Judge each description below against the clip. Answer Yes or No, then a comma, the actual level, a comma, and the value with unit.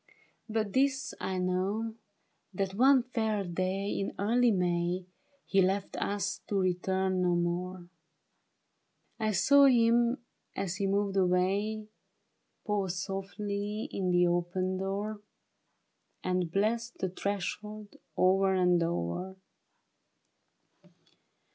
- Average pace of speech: No, slow, 105 wpm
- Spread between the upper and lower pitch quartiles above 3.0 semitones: No, narrow, 2.6 semitones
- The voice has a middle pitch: No, high, 195 Hz